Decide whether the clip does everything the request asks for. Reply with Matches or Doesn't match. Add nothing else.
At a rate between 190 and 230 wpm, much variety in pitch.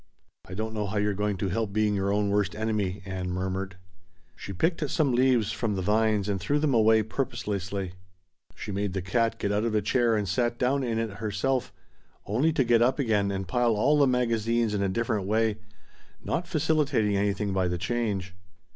Doesn't match